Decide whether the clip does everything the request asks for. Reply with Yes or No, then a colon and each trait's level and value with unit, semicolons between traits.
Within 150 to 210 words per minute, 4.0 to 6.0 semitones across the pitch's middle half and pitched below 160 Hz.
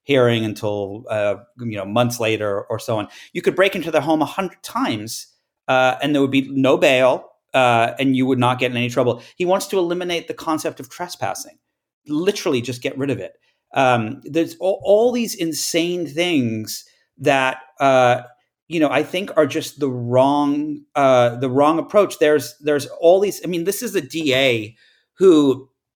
Yes: average, 185 wpm; average, 5.1 semitones; medium, 140 Hz